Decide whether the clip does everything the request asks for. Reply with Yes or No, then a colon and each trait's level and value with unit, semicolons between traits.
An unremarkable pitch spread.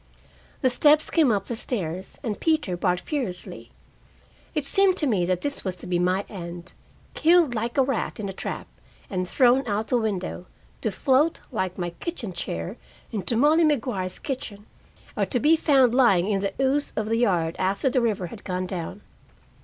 No: wide, 6.6 semitones